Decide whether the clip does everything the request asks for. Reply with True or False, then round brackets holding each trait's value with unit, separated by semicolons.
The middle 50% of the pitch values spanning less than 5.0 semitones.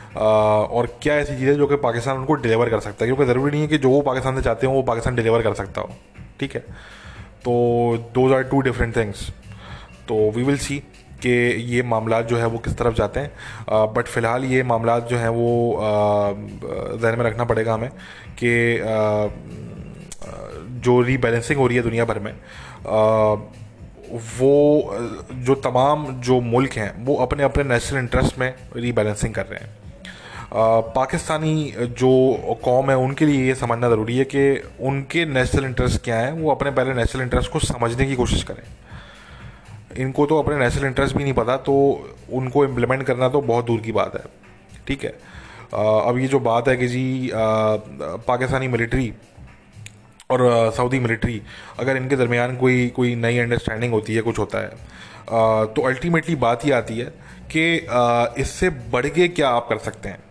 True (2.8 semitones)